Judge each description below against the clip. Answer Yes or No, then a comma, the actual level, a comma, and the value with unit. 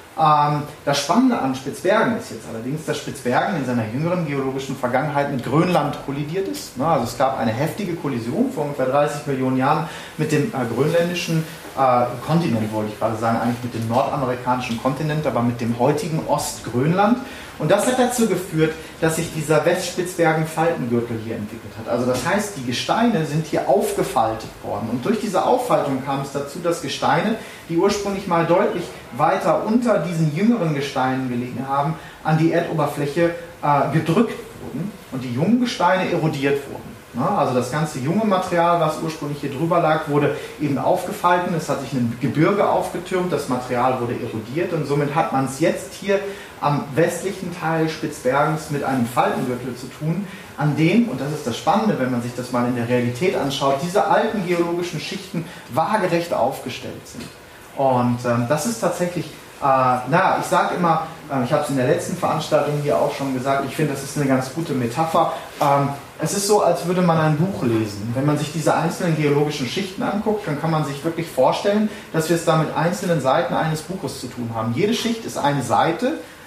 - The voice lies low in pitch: No, medium, 150 Hz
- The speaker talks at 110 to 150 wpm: No, average, 185 wpm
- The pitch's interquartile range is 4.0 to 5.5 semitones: Yes, average, 4.6 semitones